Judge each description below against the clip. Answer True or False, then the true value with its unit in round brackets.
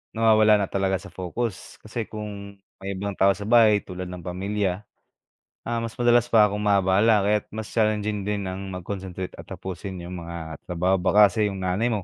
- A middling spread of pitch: False (2.3 semitones)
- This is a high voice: False (100 Hz)